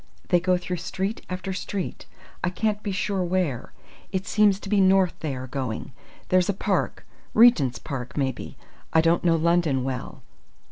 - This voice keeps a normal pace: Yes, average, 170 wpm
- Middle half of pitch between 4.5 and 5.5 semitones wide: Yes, average, 4.9 semitones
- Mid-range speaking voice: Yes, medium, 180 Hz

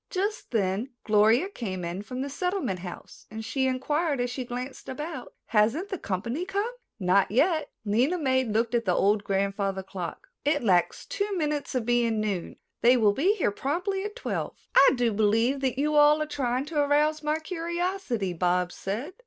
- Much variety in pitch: Yes, wide, 6.7 semitones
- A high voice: Yes, very high, 250 Hz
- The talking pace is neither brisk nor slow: Yes, average, 180 wpm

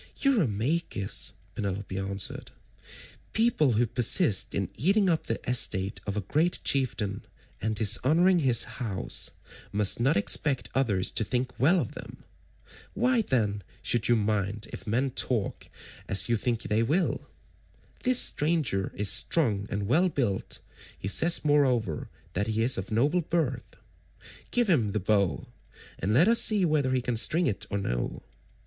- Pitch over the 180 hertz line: No, low, 120 Hz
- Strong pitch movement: Yes, wide, 7.3 semitones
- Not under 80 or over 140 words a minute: No, average, 150 wpm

